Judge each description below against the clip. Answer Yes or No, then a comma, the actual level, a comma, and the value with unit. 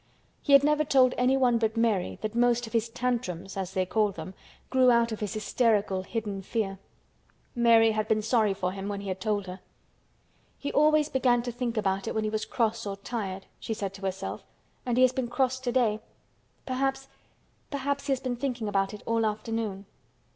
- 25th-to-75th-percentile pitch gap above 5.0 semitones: No, average, 3.8 semitones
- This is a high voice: Yes, high, 225 Hz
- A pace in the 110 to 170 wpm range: No, average, 195 wpm